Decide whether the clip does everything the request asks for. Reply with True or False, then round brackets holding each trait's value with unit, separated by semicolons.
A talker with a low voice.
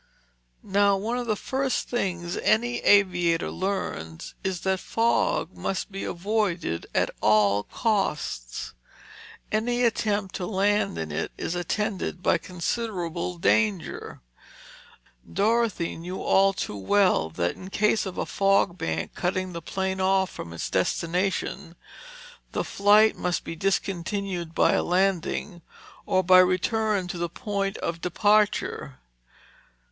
False (190 Hz)